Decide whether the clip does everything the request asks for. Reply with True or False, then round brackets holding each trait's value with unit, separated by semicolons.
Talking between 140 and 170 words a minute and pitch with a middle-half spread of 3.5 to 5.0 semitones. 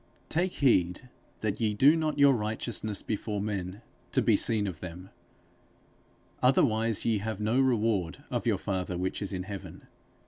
True (165 wpm; 3.8 semitones)